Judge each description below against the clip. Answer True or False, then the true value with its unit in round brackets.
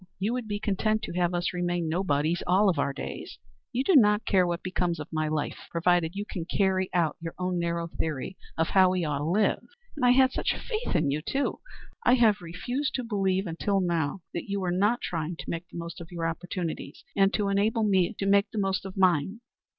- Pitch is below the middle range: False (185 Hz)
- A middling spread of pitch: True (3.4 semitones)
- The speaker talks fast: True (220 wpm)